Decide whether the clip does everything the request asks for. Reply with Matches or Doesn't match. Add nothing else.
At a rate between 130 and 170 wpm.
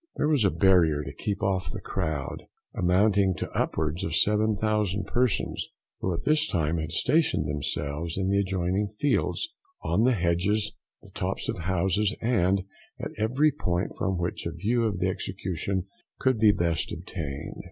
Matches